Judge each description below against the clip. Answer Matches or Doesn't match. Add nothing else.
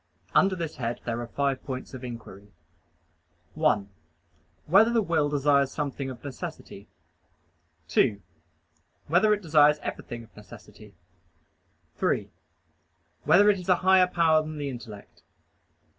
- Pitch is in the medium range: Matches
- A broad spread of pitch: Matches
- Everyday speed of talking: Doesn't match